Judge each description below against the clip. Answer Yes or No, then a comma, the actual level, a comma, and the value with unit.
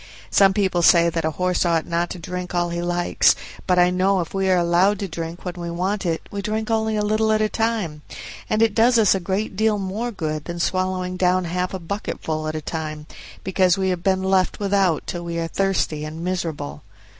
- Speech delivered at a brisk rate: Yes, fast, 225 wpm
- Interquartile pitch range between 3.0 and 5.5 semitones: No, narrow, 2.6 semitones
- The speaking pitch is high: No, medium, 180 Hz